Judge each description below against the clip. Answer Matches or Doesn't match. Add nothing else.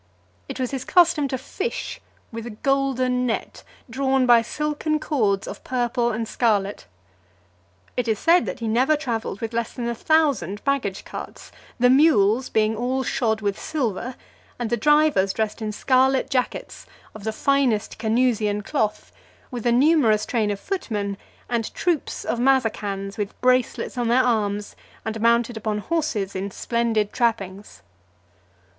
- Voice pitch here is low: Doesn't match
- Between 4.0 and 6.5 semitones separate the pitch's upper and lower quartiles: Doesn't match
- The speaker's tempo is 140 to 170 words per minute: Matches